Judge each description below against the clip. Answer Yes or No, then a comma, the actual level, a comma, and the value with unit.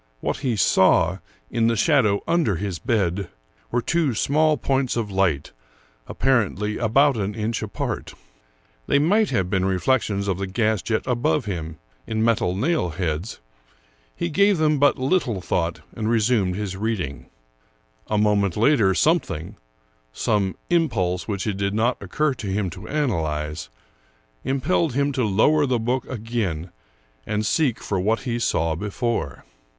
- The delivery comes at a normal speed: Yes, average, 155 wpm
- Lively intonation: Yes, wide, 5.7 semitones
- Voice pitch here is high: No, low, 110 Hz